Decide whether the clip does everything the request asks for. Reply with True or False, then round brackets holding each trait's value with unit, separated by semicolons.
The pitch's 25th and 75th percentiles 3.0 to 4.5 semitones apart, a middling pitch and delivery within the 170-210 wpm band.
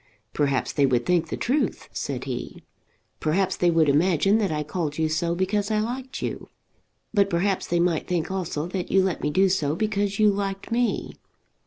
True (4.1 semitones; 180 Hz; 190 wpm)